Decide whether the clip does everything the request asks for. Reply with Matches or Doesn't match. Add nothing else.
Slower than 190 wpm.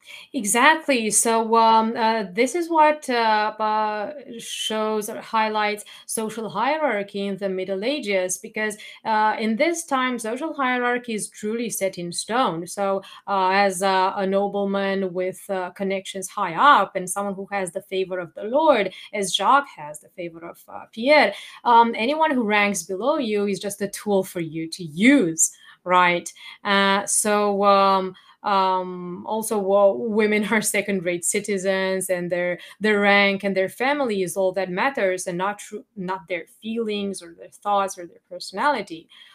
Matches